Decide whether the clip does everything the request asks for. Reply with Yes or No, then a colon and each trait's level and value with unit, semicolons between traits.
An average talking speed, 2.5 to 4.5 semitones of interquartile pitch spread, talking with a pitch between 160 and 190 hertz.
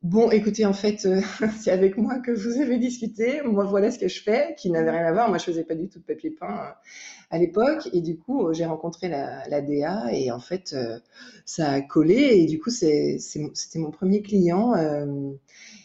No: average, 210 wpm; wide, 5.4 semitones; medium, 185 Hz